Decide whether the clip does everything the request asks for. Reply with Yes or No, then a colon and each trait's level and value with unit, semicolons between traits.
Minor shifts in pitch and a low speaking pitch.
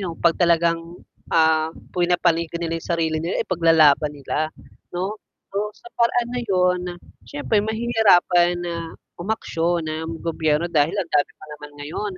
No: narrow, 2.2 semitones; medium, 170 Hz